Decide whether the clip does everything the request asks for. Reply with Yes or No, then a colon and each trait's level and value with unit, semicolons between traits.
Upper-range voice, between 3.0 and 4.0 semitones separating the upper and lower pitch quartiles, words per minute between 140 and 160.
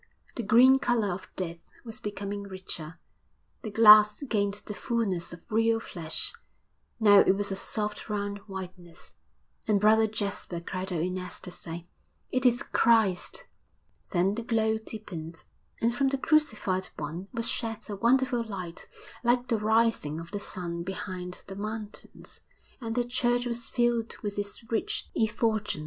Yes: high, 210 Hz; average, 3.6 semitones; average, 150 wpm